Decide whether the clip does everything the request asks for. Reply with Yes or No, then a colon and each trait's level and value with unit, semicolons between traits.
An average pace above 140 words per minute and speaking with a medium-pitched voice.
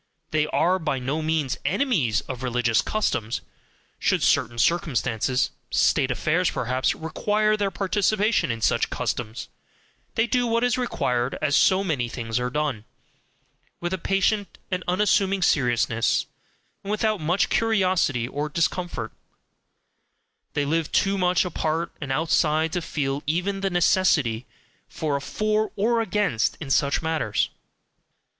No: slow, 135 wpm; medium, 160 Hz